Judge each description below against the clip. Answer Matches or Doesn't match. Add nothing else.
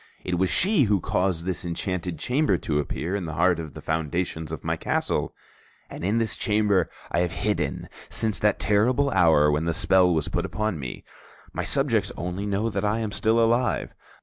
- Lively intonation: Doesn't match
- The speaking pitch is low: Matches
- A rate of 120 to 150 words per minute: Doesn't match